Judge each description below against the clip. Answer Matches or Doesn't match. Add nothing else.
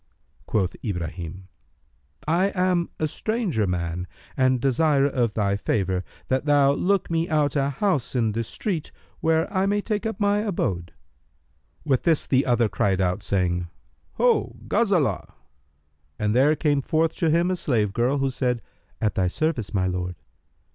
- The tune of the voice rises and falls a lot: Matches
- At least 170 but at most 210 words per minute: Doesn't match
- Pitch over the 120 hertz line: Matches